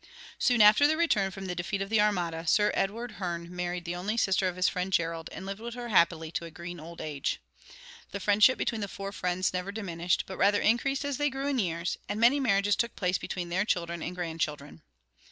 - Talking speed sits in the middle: No, fast, 225 wpm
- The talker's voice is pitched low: No, high, 190 Hz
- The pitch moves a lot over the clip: No, average, 3.7 semitones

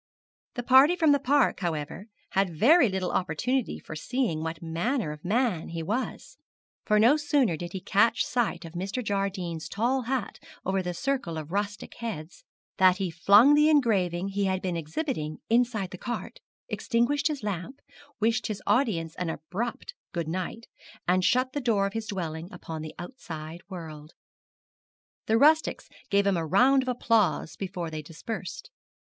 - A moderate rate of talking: Yes, average, 165 wpm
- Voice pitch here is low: No, high, 200 Hz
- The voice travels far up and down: Yes, wide, 6.3 semitones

